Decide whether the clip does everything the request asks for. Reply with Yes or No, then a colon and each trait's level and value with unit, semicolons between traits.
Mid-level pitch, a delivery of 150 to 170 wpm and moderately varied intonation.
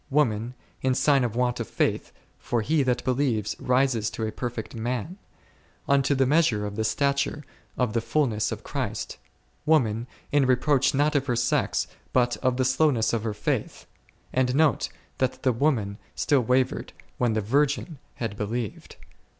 No: low, 125 Hz; average, 165 wpm; average, 3.6 semitones